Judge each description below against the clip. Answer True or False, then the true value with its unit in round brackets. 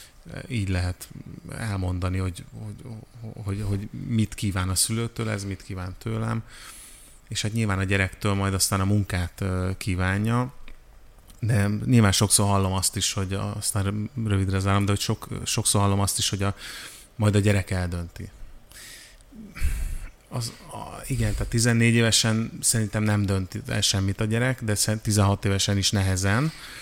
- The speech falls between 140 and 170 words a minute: True (150 wpm)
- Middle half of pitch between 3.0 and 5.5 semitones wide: False (2.6 semitones)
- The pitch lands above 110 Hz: False (105 Hz)